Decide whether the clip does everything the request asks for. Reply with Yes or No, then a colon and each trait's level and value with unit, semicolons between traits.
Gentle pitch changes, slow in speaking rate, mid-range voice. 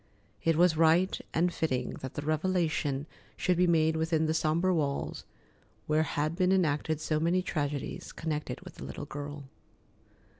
No: narrow, 2.3 semitones; average, 155 wpm; medium, 160 Hz